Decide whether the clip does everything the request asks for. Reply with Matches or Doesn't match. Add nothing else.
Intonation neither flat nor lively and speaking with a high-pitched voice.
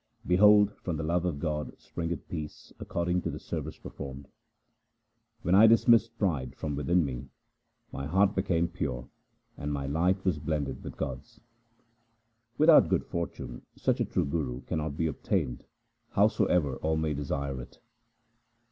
Doesn't match